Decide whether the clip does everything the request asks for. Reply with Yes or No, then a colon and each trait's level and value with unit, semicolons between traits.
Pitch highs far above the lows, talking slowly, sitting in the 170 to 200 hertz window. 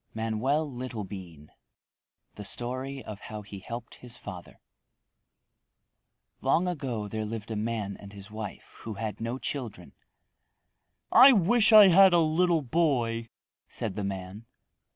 No: wide, 5.7 semitones; slow, 130 wpm; low, 115 Hz